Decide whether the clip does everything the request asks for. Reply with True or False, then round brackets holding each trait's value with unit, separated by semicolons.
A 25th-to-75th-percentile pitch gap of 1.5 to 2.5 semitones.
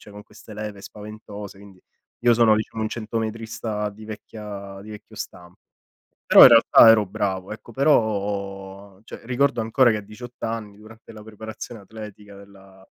True (1.9 semitones)